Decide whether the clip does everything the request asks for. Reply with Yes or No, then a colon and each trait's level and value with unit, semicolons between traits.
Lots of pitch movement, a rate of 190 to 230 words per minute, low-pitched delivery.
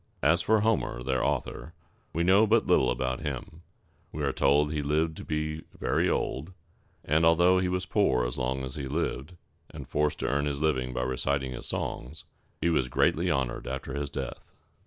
No: average, 4.1 semitones; average, 200 wpm; very low, 75 Hz